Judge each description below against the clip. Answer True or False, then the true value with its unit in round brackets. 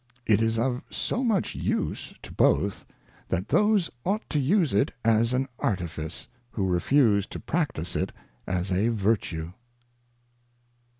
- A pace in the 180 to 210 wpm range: False (135 wpm)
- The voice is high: False (115 Hz)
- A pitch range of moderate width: False (7.3 semitones)